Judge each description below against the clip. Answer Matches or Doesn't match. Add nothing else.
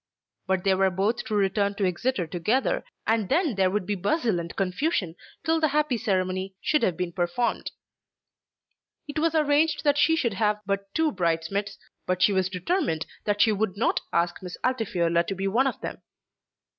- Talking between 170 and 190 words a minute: Matches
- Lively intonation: Matches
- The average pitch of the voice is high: Matches